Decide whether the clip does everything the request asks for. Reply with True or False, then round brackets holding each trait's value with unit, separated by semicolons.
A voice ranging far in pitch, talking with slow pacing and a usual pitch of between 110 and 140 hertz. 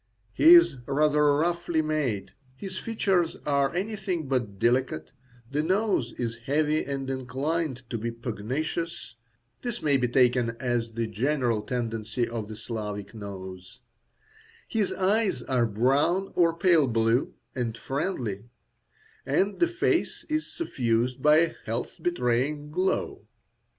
True (6.3 semitones; 130 wpm; 135 Hz)